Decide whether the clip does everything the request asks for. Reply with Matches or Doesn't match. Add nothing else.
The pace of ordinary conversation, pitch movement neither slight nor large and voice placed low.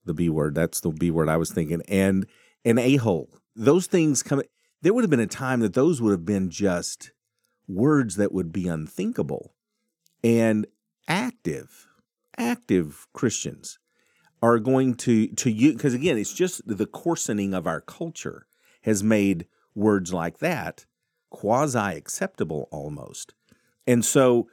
Doesn't match